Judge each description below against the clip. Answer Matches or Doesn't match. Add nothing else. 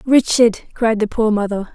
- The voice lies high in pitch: Matches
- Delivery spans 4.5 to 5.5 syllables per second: Matches